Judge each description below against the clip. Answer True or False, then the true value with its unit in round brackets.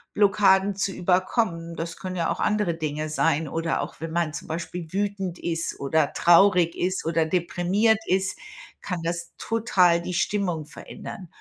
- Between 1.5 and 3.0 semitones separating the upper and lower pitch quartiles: True (2.7 semitones)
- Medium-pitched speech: True (175 Hz)